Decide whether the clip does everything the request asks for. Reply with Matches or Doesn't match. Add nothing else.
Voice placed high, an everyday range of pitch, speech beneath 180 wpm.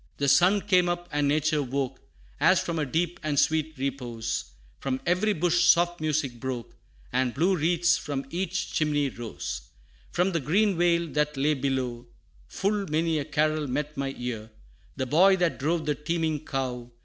Doesn't match